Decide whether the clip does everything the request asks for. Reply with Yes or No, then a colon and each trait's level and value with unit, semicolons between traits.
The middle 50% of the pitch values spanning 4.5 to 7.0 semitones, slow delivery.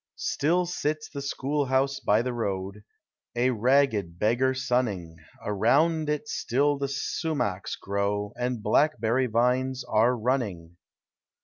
Yes: average, 4.9 semitones; slow, 120 wpm